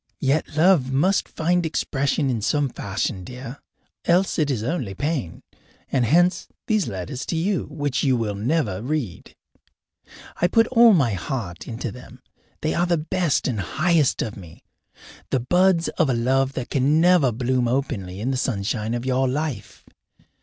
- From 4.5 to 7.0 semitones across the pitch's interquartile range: Yes, wide, 5.5 semitones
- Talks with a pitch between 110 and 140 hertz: Yes, low, 135 Hz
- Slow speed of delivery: No, average, 165 wpm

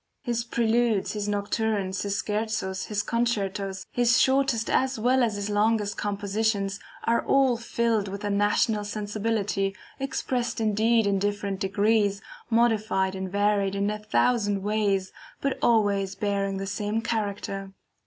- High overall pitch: Yes, high, 210 Hz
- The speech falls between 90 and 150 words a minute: Yes, slow, 135 wpm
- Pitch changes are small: Yes, narrow, 2.3 semitones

